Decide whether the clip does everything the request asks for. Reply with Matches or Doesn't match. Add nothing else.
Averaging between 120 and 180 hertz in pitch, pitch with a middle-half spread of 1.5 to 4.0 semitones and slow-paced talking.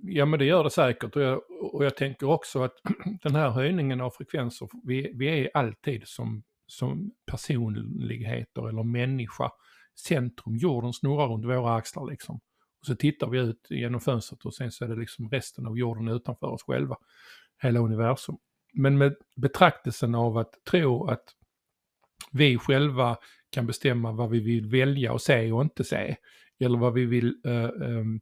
Doesn't match